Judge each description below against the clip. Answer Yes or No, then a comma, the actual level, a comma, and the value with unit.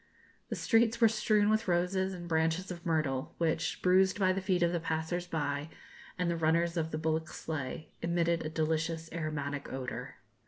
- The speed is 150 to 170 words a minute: No, average, 180 wpm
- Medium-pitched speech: Yes, medium, 170 Hz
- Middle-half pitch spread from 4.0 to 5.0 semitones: No, narrow, 2.4 semitones